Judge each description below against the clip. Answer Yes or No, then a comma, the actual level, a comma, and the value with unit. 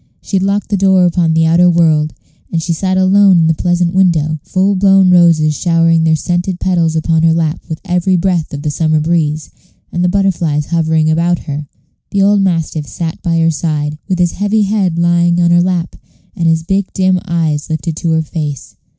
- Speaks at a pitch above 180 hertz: No, medium, 170 Hz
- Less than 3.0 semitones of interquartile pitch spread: Yes, narrow, 2.4 semitones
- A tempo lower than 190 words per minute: No, fast, 205 wpm